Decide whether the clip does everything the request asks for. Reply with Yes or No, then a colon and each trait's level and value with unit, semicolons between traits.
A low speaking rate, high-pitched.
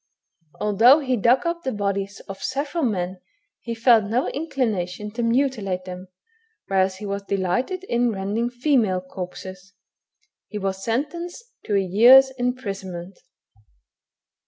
Yes: slow, 125 wpm; high, 215 Hz